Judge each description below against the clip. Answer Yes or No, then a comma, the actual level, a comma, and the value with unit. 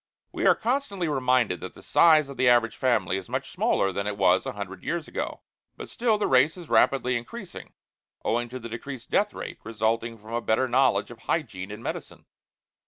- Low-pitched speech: Yes, low, 120 Hz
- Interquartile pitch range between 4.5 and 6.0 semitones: Yes, average, 5.3 semitones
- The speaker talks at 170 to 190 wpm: No, average, 200 wpm